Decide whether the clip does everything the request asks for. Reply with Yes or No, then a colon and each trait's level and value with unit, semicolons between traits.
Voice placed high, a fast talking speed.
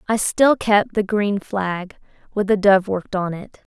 No: high, 200 Hz; average, 190 wpm